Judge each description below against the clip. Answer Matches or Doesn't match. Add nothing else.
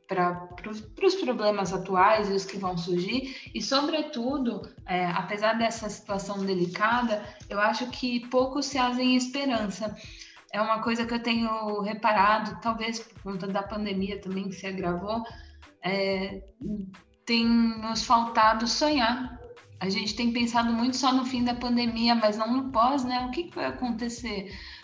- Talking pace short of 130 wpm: Doesn't match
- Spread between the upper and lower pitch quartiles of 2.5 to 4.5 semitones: Matches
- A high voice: Matches